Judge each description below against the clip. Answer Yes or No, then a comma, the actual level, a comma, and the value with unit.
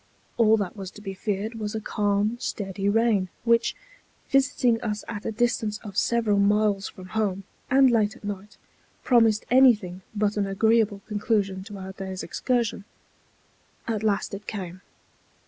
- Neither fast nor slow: Yes, average, 160 wpm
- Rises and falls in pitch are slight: Yes, narrow, 2.3 semitones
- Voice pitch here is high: Yes, high, 210 Hz